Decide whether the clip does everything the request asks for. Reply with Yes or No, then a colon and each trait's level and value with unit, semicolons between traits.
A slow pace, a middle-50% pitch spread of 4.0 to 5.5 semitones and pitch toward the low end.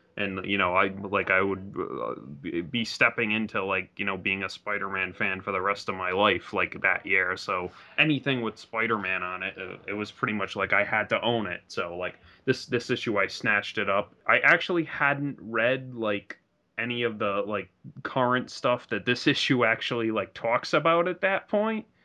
No: average, 195 wpm; average, 4.6 semitones; low, 110 Hz